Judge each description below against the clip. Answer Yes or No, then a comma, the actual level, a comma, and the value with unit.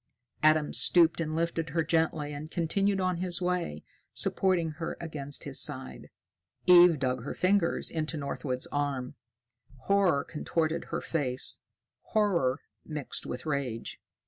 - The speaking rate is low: Yes, slow, 130 wpm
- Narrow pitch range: No, average, 3.3 semitones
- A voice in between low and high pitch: Yes, medium, 160 Hz